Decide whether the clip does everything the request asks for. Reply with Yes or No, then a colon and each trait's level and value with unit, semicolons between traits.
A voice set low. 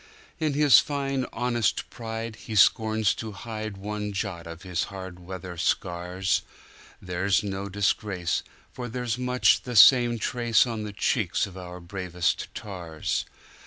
Yes: low, 105 Hz